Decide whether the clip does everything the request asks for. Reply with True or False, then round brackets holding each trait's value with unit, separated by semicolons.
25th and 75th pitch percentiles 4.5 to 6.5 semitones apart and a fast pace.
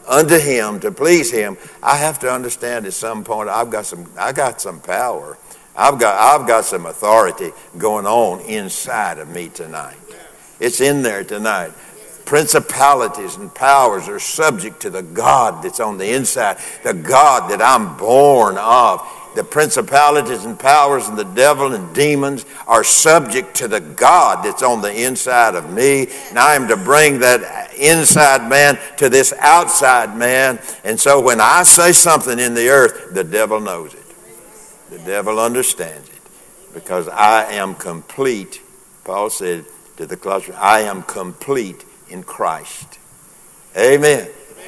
False (5.4 semitones; 155 wpm)